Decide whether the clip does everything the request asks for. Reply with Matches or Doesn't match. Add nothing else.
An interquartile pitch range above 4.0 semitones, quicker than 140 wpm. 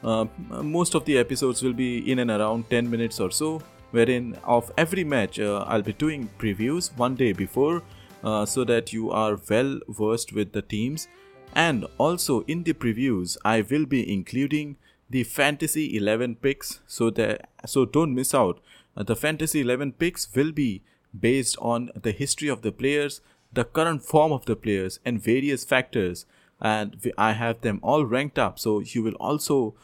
Matches